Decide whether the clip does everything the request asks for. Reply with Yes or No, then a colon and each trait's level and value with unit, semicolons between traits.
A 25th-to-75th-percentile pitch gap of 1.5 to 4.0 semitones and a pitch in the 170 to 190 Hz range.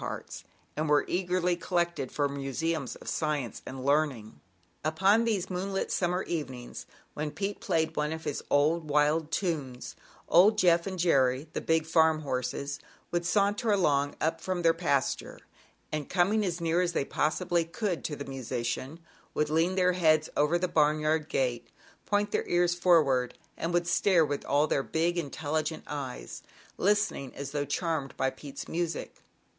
No: average, 3.5 semitones; medium, 160 Hz